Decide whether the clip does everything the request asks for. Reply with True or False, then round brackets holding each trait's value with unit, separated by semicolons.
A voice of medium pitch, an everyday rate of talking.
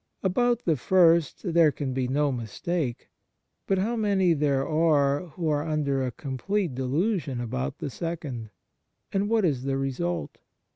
True (155 Hz; 155 wpm)